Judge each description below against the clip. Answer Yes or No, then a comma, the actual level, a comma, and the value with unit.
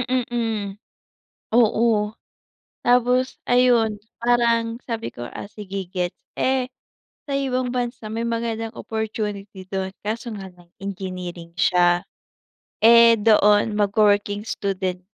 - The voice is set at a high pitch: Yes, high, 220 Hz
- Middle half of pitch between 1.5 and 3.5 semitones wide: Yes, average, 3.1 semitones